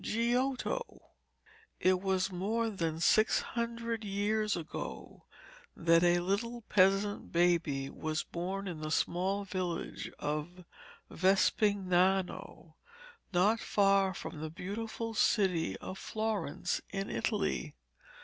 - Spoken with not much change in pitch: No, average, 3.5 semitones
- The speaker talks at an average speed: No, slow, 105 wpm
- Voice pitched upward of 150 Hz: Yes, high, 190 Hz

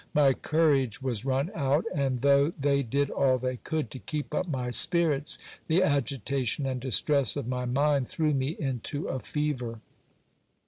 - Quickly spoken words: No, average, 165 wpm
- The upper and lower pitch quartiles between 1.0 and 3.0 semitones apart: Yes, narrow, 2.6 semitones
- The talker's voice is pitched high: No, medium, 140 Hz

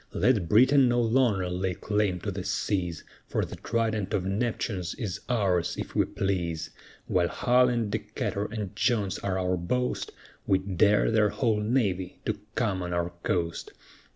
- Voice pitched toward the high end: No, low, 100 Hz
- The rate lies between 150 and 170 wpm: Yes, average, 160 wpm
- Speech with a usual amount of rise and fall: Yes, average, 3.9 semitones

